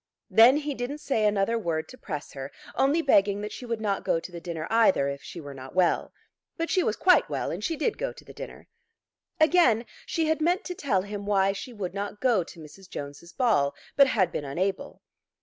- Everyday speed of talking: No, fast, 220 wpm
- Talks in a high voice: Yes, high, 205 Hz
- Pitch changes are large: Yes, wide, 7.8 semitones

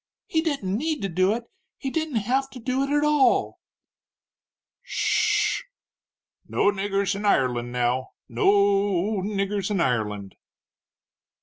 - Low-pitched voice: No, high, 200 Hz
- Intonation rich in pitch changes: Yes, wide, 6.6 semitones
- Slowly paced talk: No, average, 145 wpm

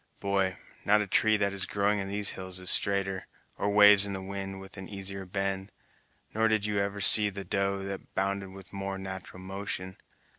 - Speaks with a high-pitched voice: No, low, 100 Hz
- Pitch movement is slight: Yes, narrow, 0.9 semitones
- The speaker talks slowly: No, average, 200 wpm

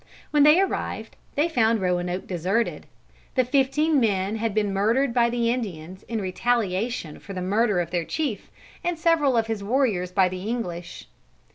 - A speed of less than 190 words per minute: Yes, average, 165 wpm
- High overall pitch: Yes, high, 225 Hz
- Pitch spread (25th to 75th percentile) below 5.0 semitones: No, wide, 5.4 semitones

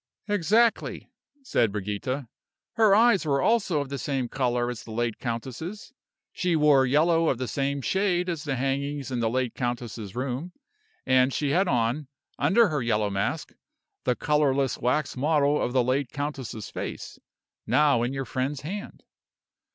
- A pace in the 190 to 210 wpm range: No, average, 160 wpm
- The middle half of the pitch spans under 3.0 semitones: No, average, 4.1 semitones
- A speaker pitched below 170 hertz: Yes, low, 135 Hz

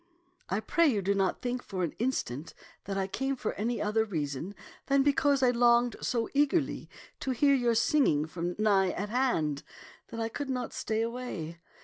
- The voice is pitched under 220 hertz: No, high, 225 Hz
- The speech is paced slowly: No, average, 185 wpm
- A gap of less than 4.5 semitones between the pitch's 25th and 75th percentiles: No, average, 5.1 semitones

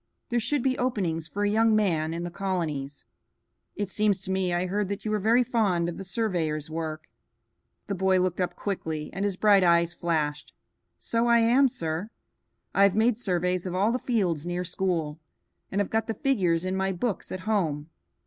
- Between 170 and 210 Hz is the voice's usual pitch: Yes, high, 190 Hz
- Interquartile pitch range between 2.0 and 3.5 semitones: No, average, 4.0 semitones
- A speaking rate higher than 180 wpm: Yes, average, 195 wpm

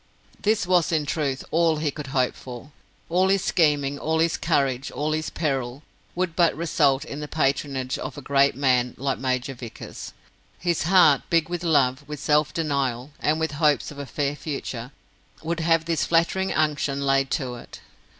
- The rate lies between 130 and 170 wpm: No, average, 180 wpm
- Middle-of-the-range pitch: Yes, medium, 150 Hz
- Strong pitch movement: No, average, 3.1 semitones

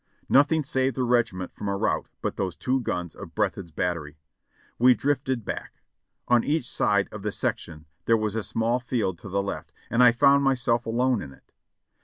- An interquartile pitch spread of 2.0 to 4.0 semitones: No, average, 4.6 semitones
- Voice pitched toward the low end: Yes, low, 115 Hz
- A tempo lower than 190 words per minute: No, average, 195 wpm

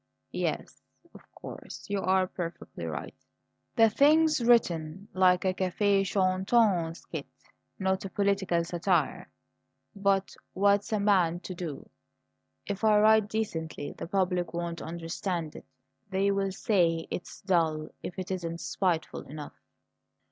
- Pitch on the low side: No, high, 190 Hz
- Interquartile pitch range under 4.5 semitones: Yes, average, 2.9 semitones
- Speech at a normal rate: No, slow, 130 wpm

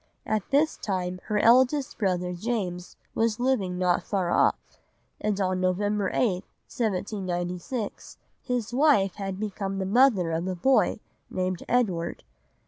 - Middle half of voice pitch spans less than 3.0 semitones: No, average, 4.1 semitones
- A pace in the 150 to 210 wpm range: No, slow, 135 wpm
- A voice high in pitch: Yes, high, 195 Hz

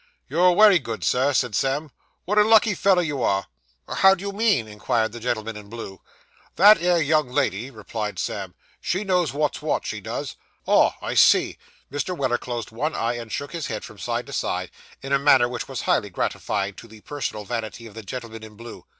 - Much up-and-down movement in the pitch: Yes, wide, 7.2 semitones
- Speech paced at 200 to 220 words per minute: Yes, fast, 205 wpm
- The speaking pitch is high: No, low, 125 Hz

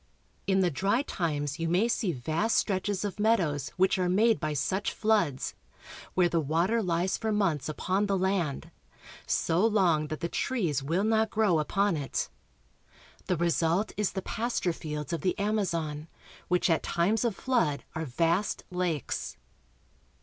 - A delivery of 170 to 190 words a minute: No, average, 155 wpm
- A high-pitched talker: No, medium, 180 Hz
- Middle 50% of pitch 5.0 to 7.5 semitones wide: No, average, 4.4 semitones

